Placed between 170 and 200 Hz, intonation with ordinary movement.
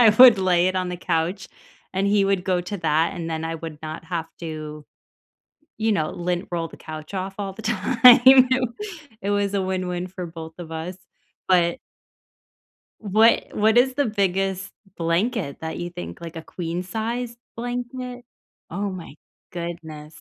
Yes: medium, 185 Hz; average, 4.0 semitones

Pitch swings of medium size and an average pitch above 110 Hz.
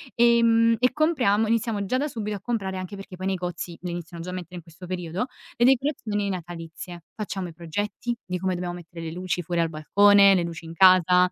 Yes: average, 3.5 semitones; medium, 185 Hz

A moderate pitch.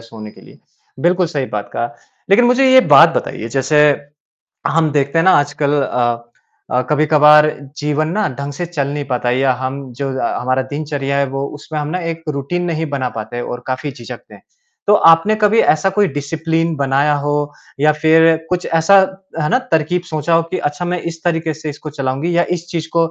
Yes: medium, 150 Hz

